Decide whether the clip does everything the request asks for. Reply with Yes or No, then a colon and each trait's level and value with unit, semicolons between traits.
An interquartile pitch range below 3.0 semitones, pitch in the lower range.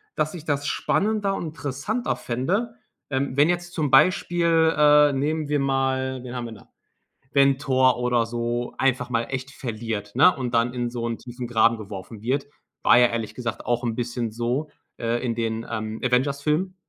No: average, 3.9 semitones; low, 130 Hz